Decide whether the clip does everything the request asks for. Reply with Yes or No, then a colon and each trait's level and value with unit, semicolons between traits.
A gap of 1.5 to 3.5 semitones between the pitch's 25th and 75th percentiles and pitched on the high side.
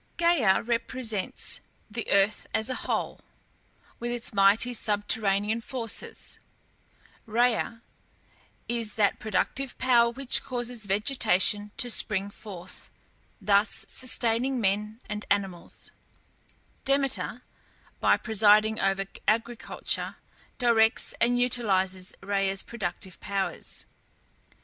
Yes: average, 3.2 semitones; high, 220 Hz